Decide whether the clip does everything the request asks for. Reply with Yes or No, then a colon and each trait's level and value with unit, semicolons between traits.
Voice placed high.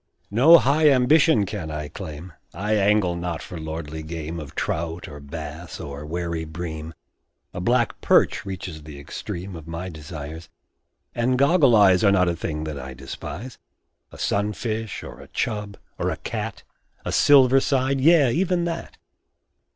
No: very low, 90 Hz